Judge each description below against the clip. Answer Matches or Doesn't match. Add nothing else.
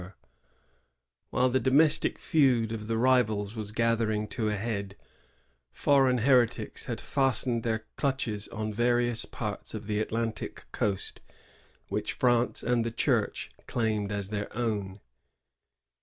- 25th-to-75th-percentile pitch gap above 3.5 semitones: Doesn't match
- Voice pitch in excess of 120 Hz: Doesn't match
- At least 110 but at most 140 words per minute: Matches